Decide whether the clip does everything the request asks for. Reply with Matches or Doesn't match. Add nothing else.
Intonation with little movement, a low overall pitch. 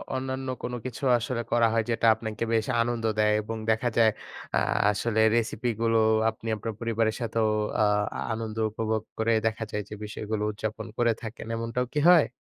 Matches